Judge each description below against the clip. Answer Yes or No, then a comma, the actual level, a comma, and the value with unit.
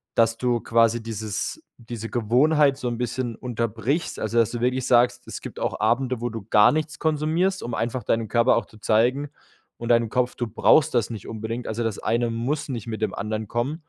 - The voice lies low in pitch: Yes, low, 120 Hz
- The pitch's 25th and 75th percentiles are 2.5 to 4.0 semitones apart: No, narrow, 2.1 semitones